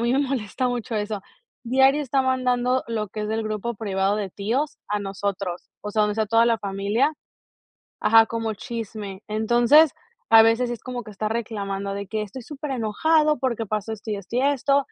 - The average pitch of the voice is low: No, high, 225 Hz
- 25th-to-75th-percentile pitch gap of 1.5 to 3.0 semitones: No, average, 3.4 semitones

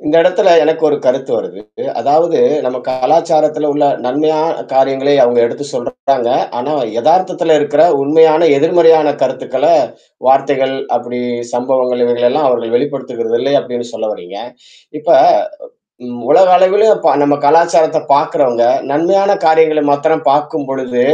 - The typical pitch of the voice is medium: Yes, medium, 145 Hz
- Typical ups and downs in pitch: Yes, average, 4.1 semitones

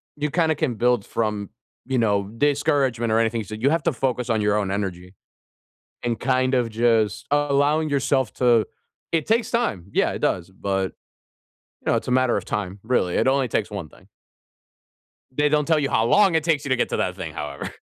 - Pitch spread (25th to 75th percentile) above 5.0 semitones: Yes, wide, 5.4 semitones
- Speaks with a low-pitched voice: Yes, low, 125 Hz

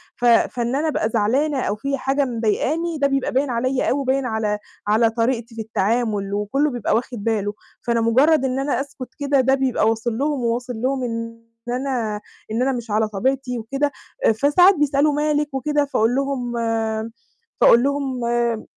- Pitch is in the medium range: No, very high, 250 Hz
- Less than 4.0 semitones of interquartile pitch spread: Yes, average, 3.3 semitones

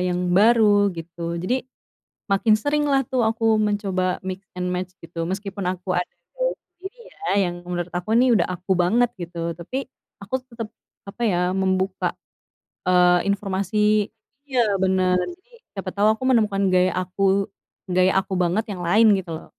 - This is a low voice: No, high, 195 Hz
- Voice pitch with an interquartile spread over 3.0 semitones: Yes, average, 3.6 semitones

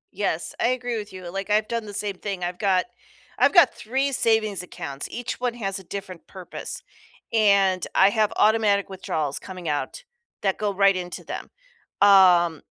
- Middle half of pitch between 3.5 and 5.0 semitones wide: No, average, 2.8 semitones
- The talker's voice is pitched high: Yes, high, 195 Hz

